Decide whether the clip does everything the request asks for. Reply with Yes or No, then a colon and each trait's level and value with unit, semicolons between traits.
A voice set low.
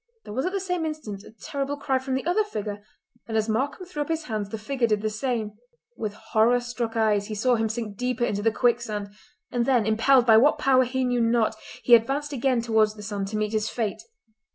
No: high, 235 Hz